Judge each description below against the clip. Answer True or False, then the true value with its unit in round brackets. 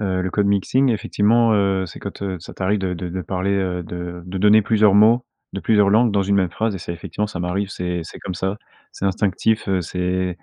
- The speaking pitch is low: True (95 Hz)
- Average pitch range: False (2.3 semitones)